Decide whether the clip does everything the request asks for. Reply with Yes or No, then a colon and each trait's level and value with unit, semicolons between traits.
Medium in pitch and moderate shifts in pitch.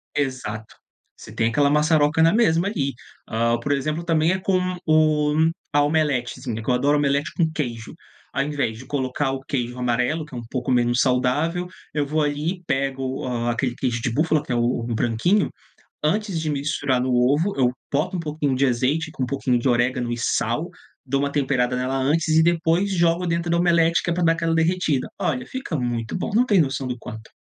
Yes: medium, 145 Hz; average, 4.4 semitones